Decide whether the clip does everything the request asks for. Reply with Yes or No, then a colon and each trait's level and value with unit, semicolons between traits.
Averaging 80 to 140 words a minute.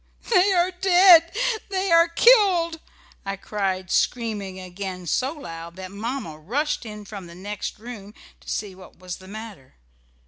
No: average, 150 wpm